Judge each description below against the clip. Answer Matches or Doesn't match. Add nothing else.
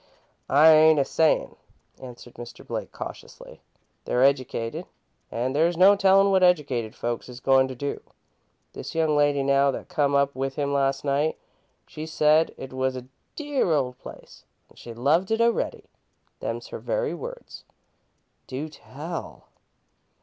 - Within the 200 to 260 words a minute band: Doesn't match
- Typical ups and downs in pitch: Matches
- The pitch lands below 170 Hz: Matches